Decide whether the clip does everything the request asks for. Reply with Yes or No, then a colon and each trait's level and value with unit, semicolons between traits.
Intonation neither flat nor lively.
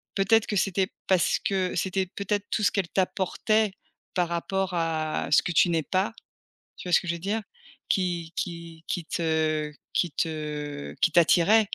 Yes: average, 3.0 semitones